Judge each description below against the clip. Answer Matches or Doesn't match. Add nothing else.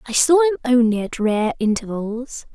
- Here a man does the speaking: Doesn't match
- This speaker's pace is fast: Doesn't match